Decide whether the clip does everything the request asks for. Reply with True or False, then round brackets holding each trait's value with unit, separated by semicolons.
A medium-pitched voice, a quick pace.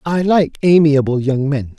False (150 Hz; 170 wpm)